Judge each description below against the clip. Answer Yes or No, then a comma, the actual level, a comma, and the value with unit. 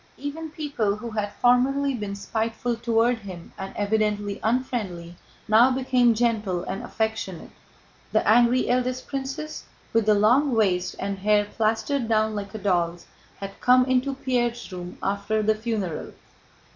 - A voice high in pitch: Yes, high, 220 Hz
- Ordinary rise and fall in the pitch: Yes, average, 3.6 semitones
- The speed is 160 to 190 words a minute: No, average, 145 wpm